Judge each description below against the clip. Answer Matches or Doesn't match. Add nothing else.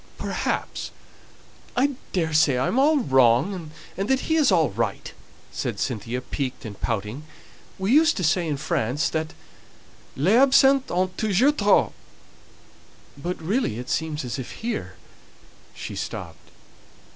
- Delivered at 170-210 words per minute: Doesn't match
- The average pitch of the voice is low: Doesn't match